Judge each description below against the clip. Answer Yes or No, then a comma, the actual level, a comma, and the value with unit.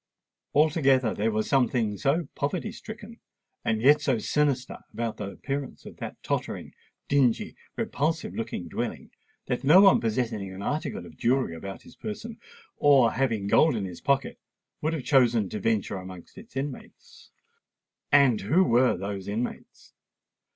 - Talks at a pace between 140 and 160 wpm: Yes, average, 150 wpm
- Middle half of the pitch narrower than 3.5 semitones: No, wide, 5.4 semitones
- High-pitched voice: No, low, 125 Hz